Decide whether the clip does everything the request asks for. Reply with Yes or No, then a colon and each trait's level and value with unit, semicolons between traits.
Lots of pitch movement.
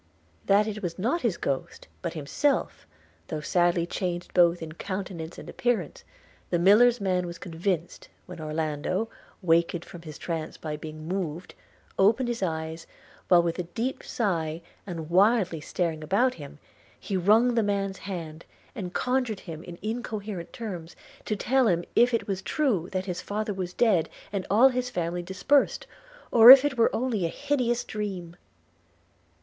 No: average, 4.9 semitones